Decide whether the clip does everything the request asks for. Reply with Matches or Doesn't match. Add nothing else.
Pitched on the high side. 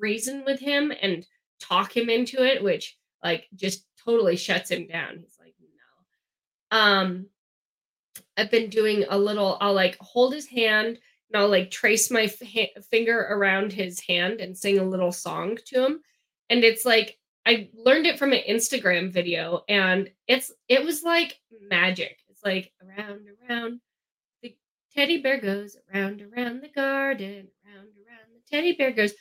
Matches